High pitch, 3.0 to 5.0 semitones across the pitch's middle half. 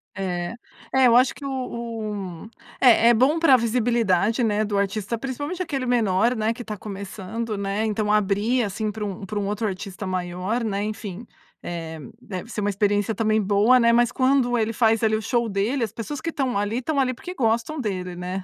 Yes: high, 220 Hz; average, 3.3 semitones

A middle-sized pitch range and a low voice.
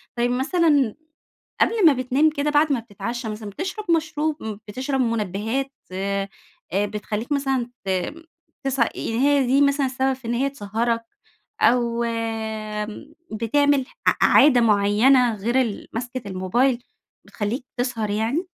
No: average, 4.1 semitones; high, 245 Hz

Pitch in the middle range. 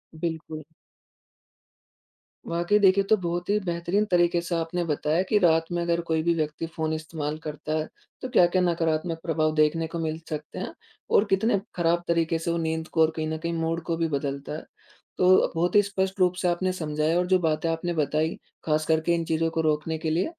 Yes: medium, 165 Hz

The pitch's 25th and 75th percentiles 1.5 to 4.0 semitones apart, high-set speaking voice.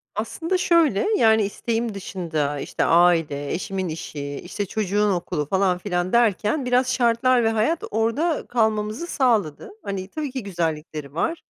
No: average, 5.2 semitones; high, 210 Hz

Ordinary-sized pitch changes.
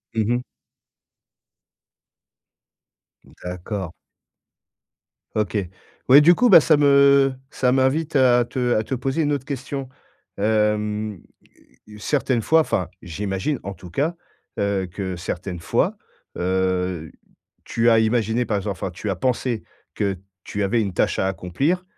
No: wide, 5.8 semitones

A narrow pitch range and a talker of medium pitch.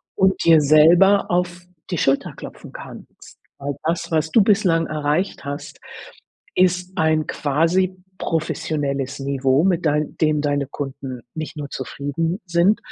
No: average, 3.7 semitones; medium, 160 Hz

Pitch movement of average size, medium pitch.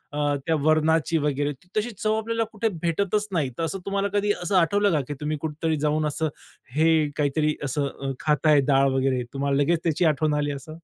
Yes: average, 3.7 semitones; medium, 155 Hz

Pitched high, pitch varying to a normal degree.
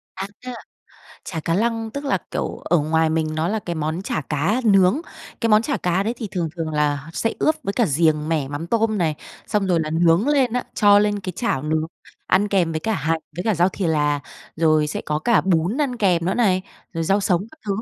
No: medium, 180 Hz; average, 5.0 semitones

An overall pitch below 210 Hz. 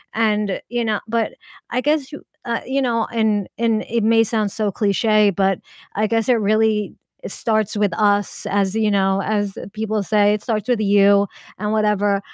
No: high, 215 Hz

